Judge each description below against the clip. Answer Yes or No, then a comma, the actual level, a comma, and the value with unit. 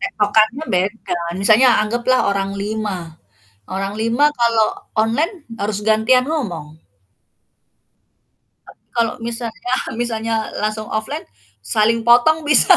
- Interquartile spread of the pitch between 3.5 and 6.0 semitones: No, average, 2.8 semitones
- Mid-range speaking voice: No, high, 220 Hz